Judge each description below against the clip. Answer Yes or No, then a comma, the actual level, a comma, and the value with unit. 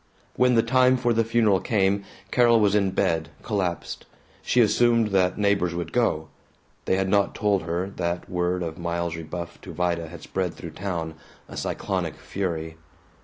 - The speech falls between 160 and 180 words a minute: Yes, average, 170 wpm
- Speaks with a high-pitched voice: No, very low, 95 Hz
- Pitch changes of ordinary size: Yes, average, 4.0 semitones